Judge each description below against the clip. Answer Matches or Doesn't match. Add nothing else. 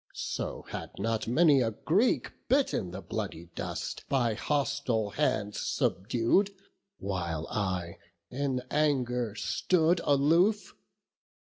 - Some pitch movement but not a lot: Doesn't match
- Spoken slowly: Matches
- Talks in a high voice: Doesn't match